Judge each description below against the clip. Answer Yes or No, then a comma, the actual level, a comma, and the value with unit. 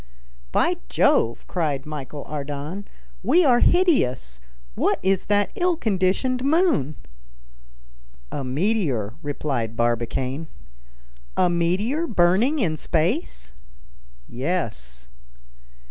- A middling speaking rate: No, slow, 90 wpm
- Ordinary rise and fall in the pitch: No, wide, 9.0 semitones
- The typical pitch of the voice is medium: Yes, medium, 165 Hz